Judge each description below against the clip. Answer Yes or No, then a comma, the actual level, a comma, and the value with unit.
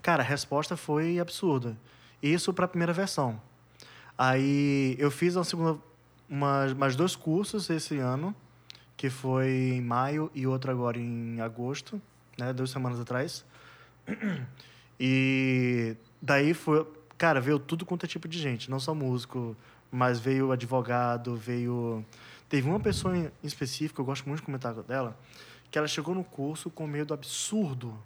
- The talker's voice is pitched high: No, low, 135 Hz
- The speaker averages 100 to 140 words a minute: No, average, 155 wpm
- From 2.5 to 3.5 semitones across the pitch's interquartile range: No, average, 4.0 semitones